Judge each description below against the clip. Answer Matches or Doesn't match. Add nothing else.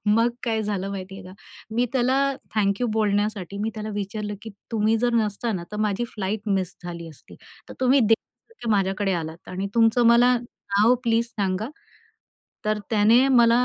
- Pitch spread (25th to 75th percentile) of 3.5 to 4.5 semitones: Doesn't match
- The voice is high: Matches